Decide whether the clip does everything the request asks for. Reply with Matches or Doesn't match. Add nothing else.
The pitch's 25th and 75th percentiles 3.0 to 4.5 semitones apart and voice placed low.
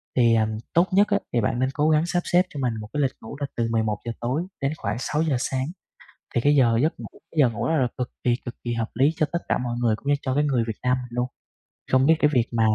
Matches